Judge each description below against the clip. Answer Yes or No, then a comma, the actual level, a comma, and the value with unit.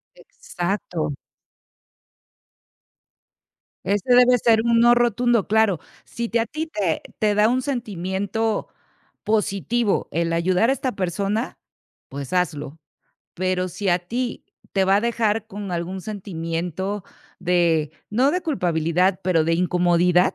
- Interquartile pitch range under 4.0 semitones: No, average, 4.6 semitones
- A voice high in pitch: Yes, high, 195 Hz